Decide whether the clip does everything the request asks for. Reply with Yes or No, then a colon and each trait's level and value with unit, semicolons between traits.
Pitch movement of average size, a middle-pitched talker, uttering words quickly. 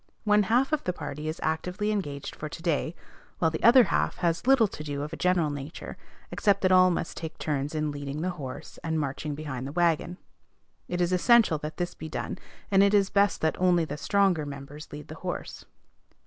Yes: average, 3.8 semitones; medium, 165 Hz; fast, 210 wpm